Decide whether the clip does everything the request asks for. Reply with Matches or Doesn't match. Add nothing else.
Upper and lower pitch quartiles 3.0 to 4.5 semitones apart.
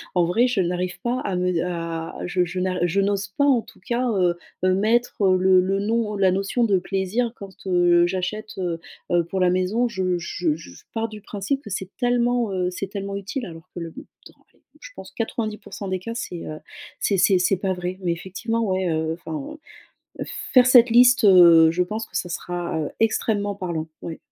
Matches